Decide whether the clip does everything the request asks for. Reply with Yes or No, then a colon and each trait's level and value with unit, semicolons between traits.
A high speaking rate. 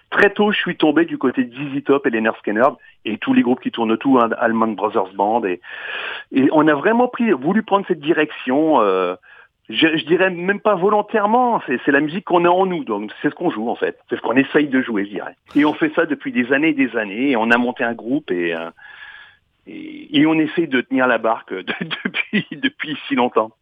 Yes: fast, 240 wpm